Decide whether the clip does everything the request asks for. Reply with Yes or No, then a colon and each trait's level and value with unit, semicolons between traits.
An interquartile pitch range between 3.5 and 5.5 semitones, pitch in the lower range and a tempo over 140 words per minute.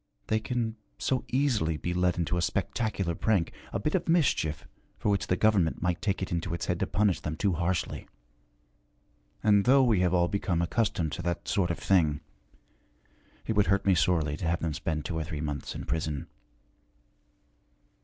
Yes: average, 4.1 semitones; very low, 90 Hz; average, 185 wpm